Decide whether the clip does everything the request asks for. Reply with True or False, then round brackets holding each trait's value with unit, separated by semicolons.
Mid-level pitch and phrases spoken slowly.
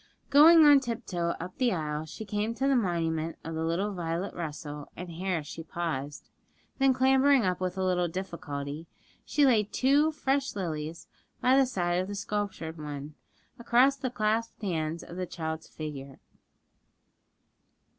False (180 Hz; 155 wpm)